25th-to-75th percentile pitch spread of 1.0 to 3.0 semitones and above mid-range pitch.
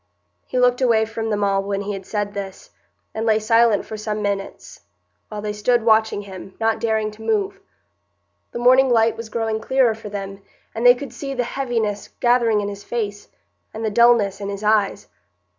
Yes: narrow, 2.6 semitones; high, 220 Hz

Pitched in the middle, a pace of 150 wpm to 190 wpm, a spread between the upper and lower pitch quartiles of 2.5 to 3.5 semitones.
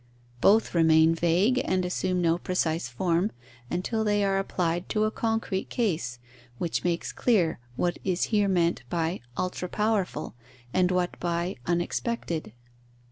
No: medium, 180 Hz; slow, 135 wpm; average, 3.2 semitones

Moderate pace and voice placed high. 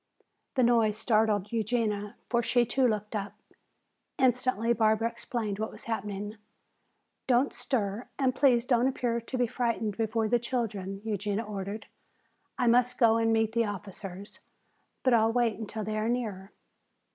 Yes: average, 150 wpm; high, 225 Hz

